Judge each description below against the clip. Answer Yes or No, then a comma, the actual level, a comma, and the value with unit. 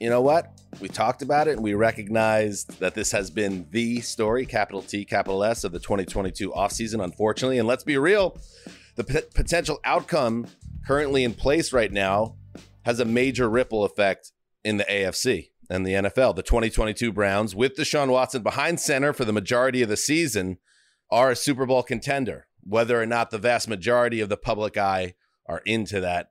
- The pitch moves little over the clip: No, average, 4.0 semitones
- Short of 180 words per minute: No, average, 185 wpm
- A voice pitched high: No, low, 115 Hz